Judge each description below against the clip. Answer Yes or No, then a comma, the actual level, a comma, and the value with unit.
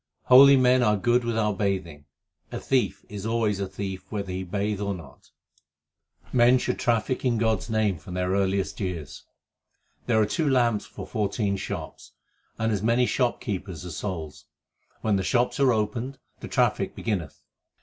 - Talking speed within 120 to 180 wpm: Yes, average, 170 wpm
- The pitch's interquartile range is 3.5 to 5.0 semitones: Yes, average, 3.8 semitones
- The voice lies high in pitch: No, low, 105 Hz